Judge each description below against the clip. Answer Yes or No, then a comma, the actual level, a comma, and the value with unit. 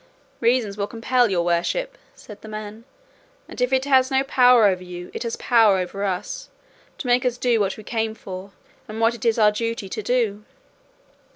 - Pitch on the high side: Yes, high, 225 Hz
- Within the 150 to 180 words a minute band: No, average, 195 wpm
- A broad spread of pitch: No, average, 3.6 semitones